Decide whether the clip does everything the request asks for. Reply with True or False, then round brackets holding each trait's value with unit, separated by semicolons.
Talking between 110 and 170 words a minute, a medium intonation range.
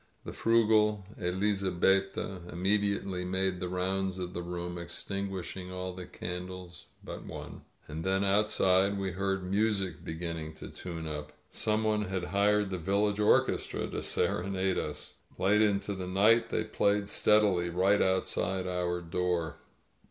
False (145 wpm; 2.0 semitones)